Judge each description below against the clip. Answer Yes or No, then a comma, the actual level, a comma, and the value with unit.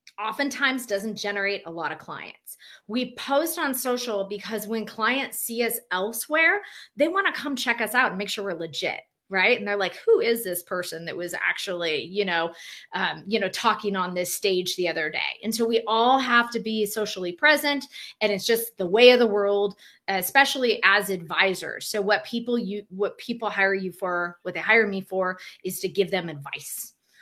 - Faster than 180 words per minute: Yes, average, 200 wpm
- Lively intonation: No, average, 4.2 semitones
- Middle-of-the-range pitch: No, high, 210 Hz